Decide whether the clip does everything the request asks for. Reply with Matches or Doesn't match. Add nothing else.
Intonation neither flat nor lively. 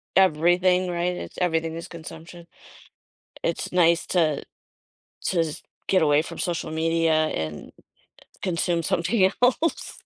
Doesn't match